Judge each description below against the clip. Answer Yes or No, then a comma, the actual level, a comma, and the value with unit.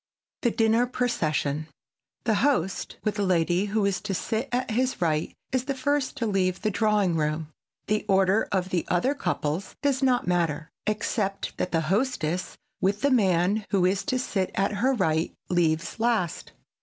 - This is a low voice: No, high, 200 Hz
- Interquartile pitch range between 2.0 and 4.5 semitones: No, average, 5.2 semitones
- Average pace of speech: Yes, average, 175 wpm